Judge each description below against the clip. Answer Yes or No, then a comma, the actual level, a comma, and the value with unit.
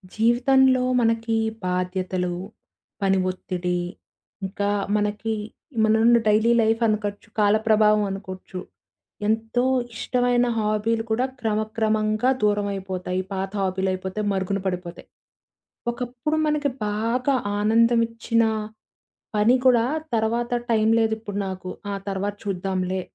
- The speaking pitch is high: Yes, high, 215 Hz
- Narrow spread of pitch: No, average, 3.1 semitones